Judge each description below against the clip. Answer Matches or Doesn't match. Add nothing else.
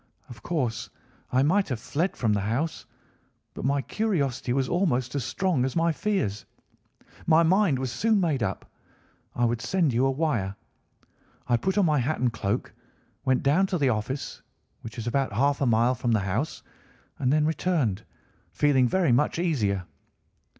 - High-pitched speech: Doesn't match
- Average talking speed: Matches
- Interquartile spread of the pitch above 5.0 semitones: Matches